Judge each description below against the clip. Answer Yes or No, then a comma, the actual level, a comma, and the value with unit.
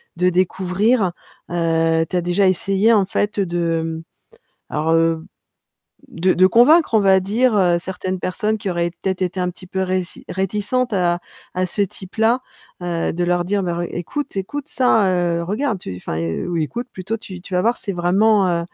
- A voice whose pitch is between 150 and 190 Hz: Yes, medium, 185 Hz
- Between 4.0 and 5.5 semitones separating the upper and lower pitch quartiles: No, average, 2.9 semitones